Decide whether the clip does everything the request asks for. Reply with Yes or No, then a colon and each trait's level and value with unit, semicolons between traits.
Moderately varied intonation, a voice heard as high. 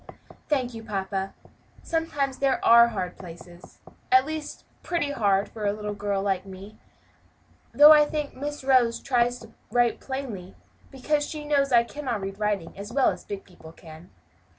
No: wide, 5.9 semitones; high, 235 Hz